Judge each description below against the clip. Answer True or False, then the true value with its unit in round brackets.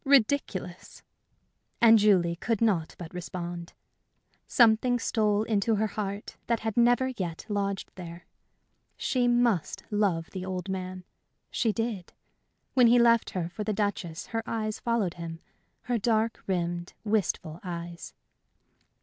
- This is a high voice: True (205 Hz)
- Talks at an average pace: False (130 wpm)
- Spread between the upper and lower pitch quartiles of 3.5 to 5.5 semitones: True (4.4 semitones)